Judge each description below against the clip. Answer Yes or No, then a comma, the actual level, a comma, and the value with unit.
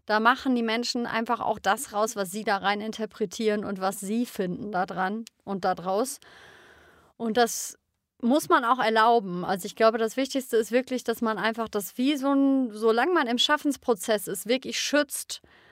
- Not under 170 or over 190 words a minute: Yes, average, 180 wpm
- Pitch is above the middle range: Yes, high, 225 Hz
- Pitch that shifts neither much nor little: Yes, average, 3.3 semitones